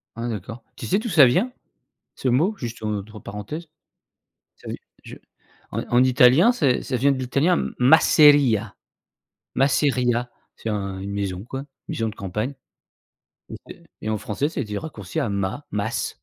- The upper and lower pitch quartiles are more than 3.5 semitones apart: Yes, average, 5.2 semitones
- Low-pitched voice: Yes, low, 120 Hz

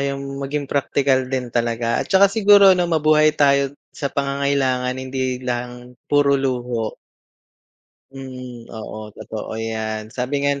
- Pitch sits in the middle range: No, low, 130 Hz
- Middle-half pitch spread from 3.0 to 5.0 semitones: No, narrow, 2.5 semitones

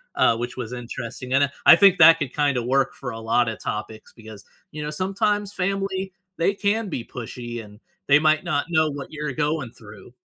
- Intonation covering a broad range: Yes, wide, 5.9 semitones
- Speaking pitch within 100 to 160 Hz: Yes, medium, 140 Hz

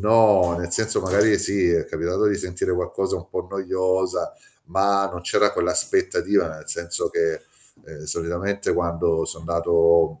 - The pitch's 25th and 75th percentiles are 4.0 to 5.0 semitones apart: No, average, 2.9 semitones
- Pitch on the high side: No, very low, 95 Hz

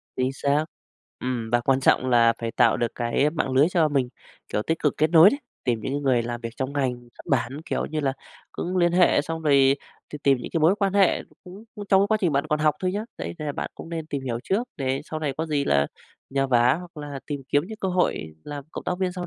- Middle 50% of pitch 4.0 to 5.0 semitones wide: Yes, average, 4.7 semitones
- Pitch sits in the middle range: Yes, medium, 145 Hz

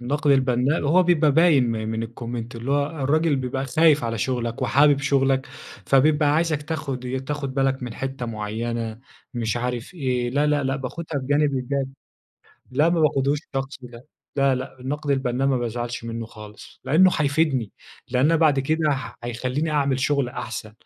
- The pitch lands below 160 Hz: Yes, low, 135 Hz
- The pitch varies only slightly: No, average, 3.2 semitones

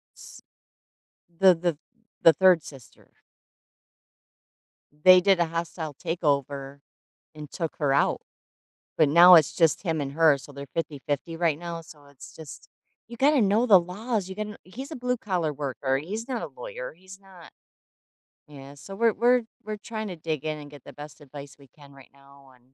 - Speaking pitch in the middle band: Yes, medium, 165 Hz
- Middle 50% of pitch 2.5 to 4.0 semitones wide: No, average, 5.2 semitones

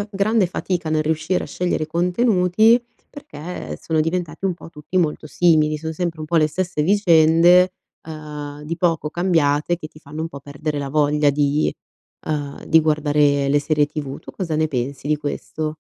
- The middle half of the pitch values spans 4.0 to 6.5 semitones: No, average, 2.8 semitones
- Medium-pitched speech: Yes, medium, 155 Hz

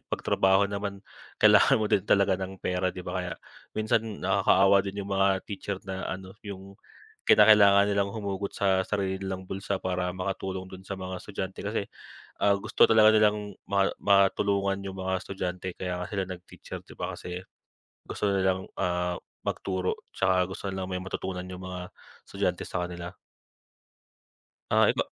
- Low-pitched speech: Yes, very low, 95 Hz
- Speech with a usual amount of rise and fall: No, narrow, 1.4 semitones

